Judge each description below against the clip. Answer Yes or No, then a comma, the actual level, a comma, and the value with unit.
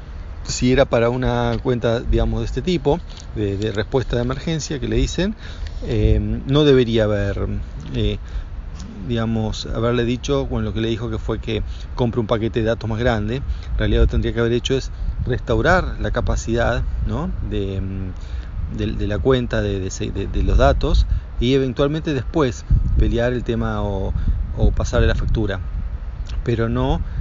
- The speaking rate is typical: Yes, average, 170 wpm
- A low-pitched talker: Yes, low, 110 Hz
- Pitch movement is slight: No, average, 3.6 semitones